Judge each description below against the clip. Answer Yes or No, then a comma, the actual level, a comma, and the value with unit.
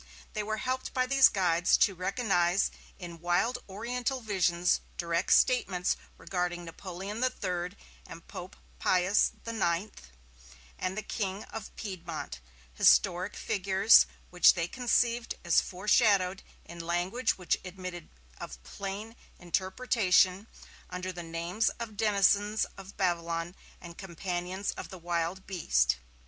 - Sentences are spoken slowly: Yes, slow, 120 wpm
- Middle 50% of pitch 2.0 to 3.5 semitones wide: Yes, average, 3.2 semitones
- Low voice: No, medium, 185 Hz